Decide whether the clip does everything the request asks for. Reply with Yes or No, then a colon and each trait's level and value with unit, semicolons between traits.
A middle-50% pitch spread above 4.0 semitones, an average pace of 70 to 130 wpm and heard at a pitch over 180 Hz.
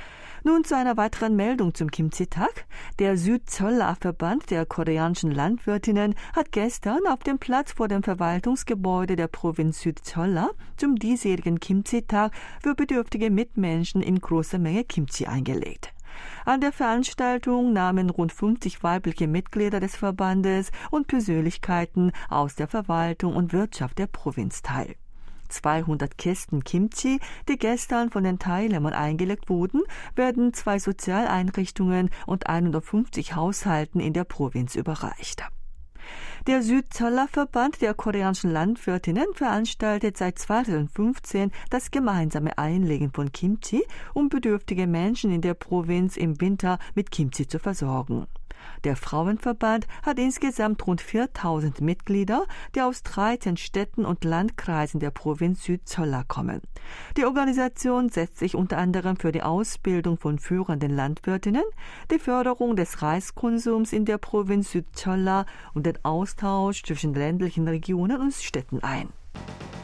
Yes: wide, 5.5 semitones; slow, 125 wpm; high, 190 Hz